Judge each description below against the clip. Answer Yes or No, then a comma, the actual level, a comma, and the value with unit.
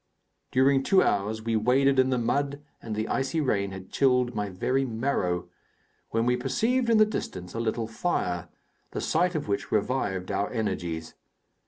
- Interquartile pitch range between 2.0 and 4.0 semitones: No, average, 5.1 semitones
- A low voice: Yes, low, 120 Hz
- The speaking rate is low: No, average, 170 wpm